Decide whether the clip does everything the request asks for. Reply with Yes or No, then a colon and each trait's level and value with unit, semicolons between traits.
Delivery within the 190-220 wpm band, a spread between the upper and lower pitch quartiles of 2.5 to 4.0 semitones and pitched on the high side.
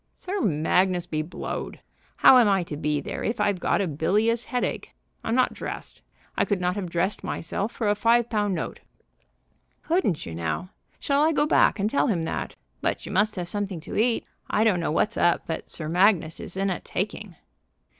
No: average, 200 wpm; average, 4.4 semitones; high, 195 Hz